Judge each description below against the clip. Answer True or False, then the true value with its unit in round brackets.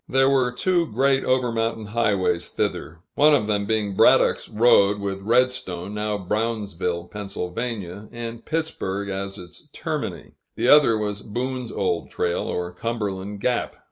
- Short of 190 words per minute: True (140 wpm)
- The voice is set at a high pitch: False (105 Hz)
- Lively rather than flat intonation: False (3.9 semitones)